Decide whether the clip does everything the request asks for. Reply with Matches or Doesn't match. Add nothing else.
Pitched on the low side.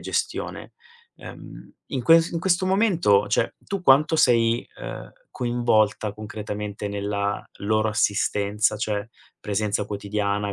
Matches